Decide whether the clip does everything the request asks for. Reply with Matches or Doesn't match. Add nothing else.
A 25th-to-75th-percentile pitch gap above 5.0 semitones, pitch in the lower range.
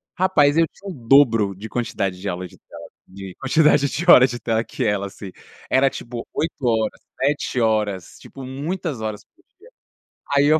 Matches